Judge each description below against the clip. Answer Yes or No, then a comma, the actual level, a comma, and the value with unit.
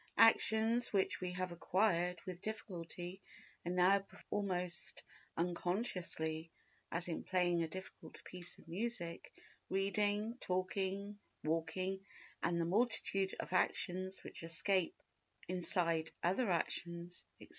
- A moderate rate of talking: No, slow, 120 wpm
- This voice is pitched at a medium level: Yes, medium, 180 Hz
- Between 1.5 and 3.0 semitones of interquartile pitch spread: Yes, narrow, 2.4 semitones